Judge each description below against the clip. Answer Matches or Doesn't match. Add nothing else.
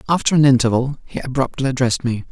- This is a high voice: Doesn't match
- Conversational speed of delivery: Matches